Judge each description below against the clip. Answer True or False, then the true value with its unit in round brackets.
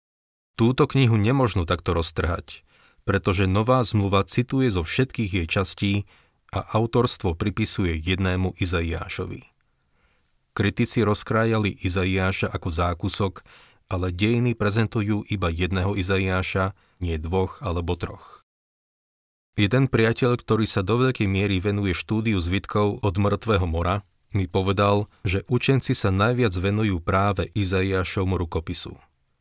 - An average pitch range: True (3.0 semitones)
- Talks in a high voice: False (100 Hz)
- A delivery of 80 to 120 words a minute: True (115 wpm)